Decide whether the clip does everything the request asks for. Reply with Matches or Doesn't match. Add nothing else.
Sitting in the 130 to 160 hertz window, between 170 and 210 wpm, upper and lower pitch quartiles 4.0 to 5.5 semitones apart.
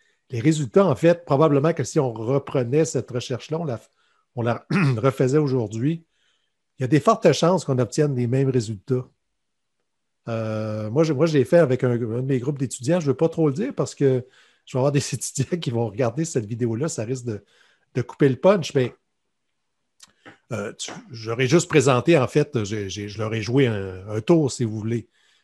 Matches